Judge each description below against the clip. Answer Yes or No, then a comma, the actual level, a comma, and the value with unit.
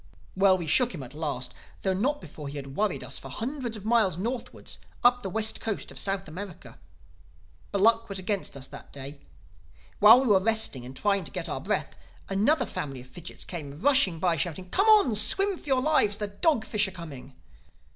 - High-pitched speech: Yes, high, 200 Hz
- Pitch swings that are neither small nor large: No, wide, 6.1 semitones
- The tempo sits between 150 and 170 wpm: No, average, 200 wpm